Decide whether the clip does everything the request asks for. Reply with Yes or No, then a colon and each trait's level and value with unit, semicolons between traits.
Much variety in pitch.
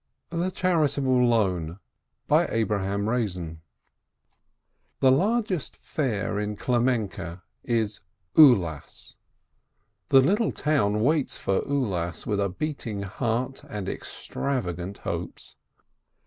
Yes: wide, 5.9 semitones